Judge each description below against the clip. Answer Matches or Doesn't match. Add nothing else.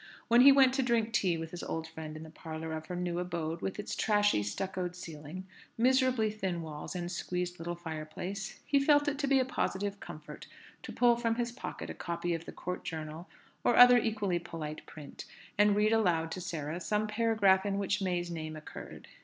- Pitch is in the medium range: Matches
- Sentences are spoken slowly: Doesn't match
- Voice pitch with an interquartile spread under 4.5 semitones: Doesn't match